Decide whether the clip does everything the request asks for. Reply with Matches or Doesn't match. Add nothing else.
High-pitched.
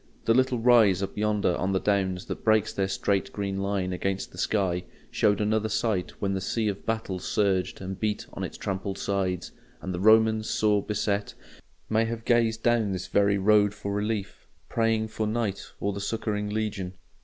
Doesn't match